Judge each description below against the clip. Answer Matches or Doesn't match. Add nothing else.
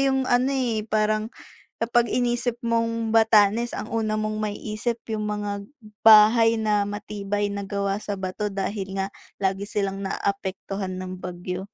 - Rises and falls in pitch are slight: Matches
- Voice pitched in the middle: Doesn't match